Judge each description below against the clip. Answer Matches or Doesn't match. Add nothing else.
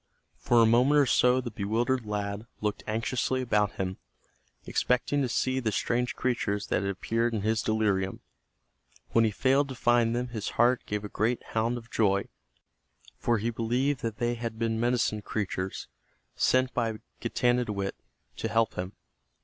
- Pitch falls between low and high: Doesn't match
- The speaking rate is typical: Matches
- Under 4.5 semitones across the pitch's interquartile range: Matches